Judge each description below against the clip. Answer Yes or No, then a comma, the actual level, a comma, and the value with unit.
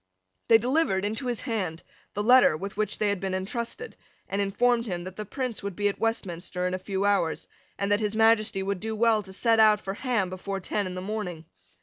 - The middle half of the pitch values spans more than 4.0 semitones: No, average, 3.0 semitones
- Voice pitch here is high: Yes, high, 205 Hz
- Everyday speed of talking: No, fast, 225 wpm